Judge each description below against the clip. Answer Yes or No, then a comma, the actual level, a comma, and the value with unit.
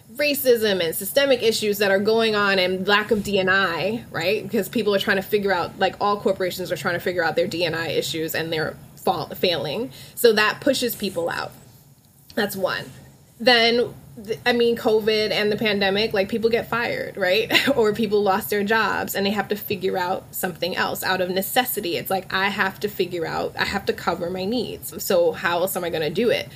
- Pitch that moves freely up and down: No, average, 3.2 semitones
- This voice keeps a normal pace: No, fast, 210 wpm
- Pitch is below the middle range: No, high, 205 Hz